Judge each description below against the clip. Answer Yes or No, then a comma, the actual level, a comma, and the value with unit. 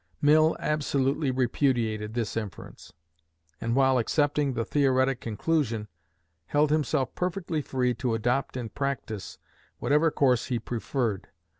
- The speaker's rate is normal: No, slow, 120 wpm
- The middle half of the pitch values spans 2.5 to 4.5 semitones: Yes, average, 4.0 semitones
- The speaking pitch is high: No, low, 130 Hz